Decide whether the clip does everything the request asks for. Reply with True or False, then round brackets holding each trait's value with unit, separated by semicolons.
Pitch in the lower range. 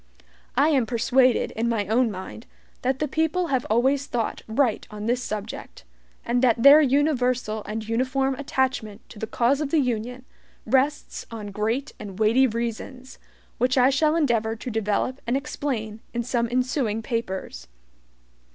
False (245 Hz)